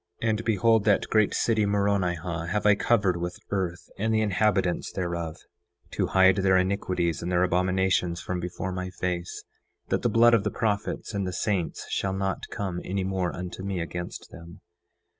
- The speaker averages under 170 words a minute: No, average, 180 wpm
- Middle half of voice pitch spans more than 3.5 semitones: No, narrow, 2.5 semitones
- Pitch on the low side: Yes, very low, 95 Hz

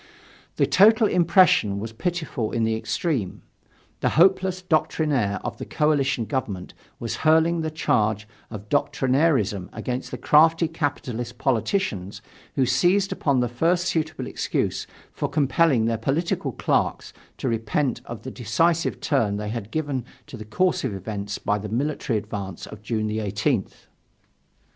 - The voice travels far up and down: Yes, wide, 6.7 semitones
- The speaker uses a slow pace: No, average, 145 wpm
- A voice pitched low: Yes, low, 130 Hz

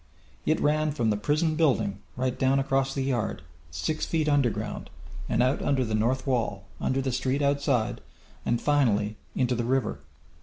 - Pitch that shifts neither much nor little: Yes, average, 3.6 semitones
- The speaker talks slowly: No, average, 175 wpm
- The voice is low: Yes, low, 130 Hz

